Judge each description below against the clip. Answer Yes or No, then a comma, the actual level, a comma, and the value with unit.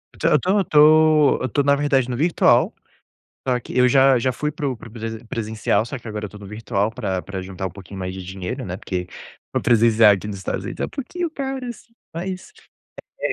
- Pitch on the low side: Yes, low, 120 Hz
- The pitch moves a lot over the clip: Yes, wide, 6.3 semitones